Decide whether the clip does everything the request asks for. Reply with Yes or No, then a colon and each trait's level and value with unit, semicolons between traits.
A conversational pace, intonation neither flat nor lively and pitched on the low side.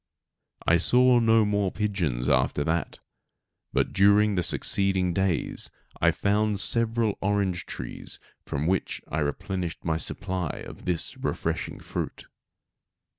No: slow, 125 wpm; average, 3.5 semitones; very low, 95 Hz